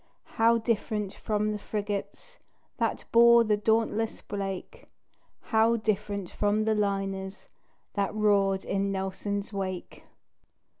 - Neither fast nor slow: No, slow, 110 wpm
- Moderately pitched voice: No, high, 210 Hz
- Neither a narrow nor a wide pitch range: No, narrow, 2.0 semitones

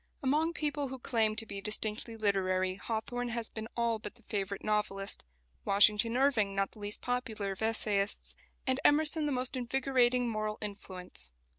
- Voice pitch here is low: No, high, 220 Hz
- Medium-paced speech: Yes, average, 160 wpm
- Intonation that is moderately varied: Yes, average, 3.5 semitones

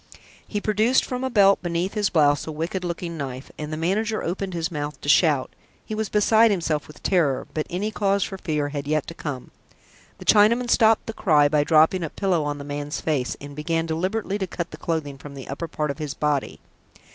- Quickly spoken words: Yes, fast, 215 wpm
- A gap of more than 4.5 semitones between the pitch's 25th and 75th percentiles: Yes, average, 5.1 semitones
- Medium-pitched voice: Yes, medium, 165 Hz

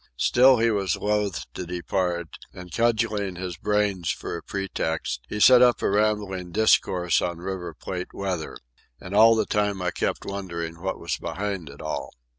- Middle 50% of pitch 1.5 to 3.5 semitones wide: Yes, average, 3.0 semitones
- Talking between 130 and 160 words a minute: No, average, 170 wpm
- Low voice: Yes, very low, 95 Hz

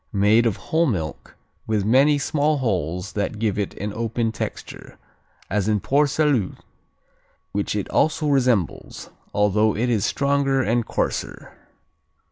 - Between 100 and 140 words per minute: Yes, slow, 135 wpm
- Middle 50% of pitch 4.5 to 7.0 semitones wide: Yes, average, 5.2 semitones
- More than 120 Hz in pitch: No, low, 115 Hz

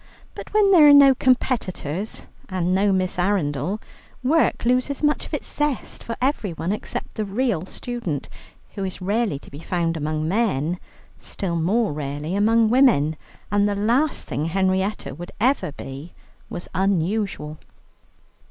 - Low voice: No, high, 195 Hz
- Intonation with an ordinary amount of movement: No, wide, 6.2 semitones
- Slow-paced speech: No, average, 145 wpm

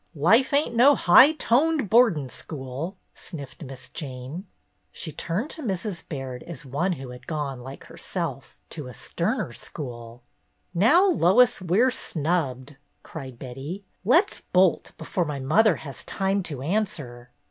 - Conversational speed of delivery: Yes, average, 150 wpm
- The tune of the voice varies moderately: No, wide, 8.0 semitones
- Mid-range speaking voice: Yes, medium, 165 Hz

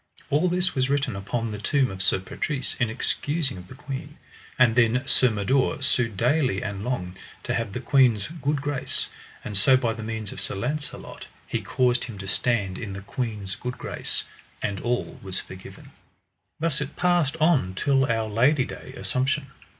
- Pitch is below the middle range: Yes, low, 125 Hz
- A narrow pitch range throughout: No, average, 5.1 semitones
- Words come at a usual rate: Yes, average, 180 wpm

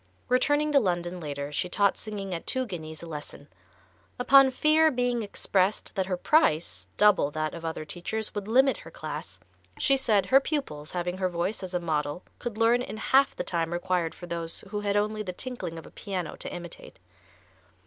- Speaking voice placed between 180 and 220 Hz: Yes, high, 190 Hz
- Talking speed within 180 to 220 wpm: Yes, average, 190 wpm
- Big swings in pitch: Yes, wide, 6.2 semitones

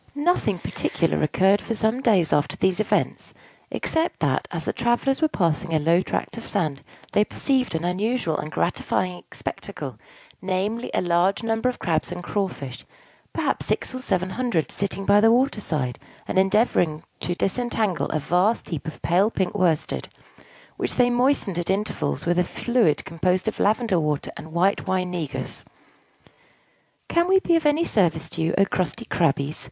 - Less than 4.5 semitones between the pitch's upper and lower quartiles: No, wide, 5.5 semitones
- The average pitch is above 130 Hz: Yes, high, 190 Hz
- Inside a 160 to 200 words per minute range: Yes, average, 170 wpm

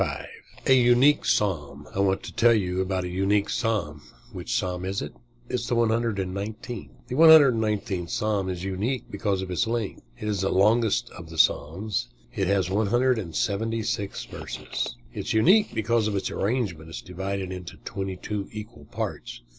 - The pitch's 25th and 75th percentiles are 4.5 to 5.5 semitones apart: No, average, 3.6 semitones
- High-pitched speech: No, low, 100 Hz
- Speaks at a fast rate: No, average, 185 wpm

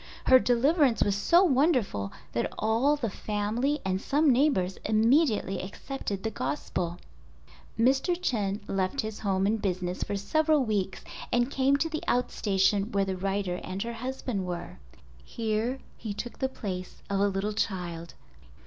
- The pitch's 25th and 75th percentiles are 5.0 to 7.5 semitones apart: Yes, average, 5.3 semitones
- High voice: Yes, high, 215 Hz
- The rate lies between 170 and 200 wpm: No, average, 155 wpm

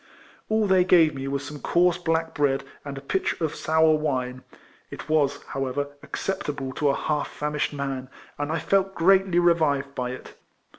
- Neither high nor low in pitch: Yes, medium, 150 Hz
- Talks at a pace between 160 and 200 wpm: Yes, average, 170 wpm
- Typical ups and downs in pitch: Yes, average, 3.6 semitones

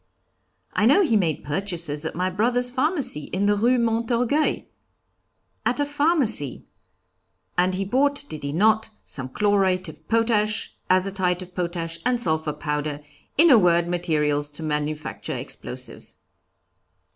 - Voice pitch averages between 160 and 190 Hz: Yes, medium, 185 Hz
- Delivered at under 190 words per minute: Yes, slow, 135 wpm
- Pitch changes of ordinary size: No, wide, 6.7 semitones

